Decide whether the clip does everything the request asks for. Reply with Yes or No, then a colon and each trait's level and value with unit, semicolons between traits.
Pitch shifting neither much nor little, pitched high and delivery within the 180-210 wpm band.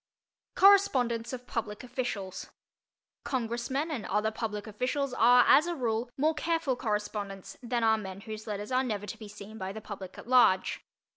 No: average, 3.5 semitones; high, 230 Hz; average, 165 wpm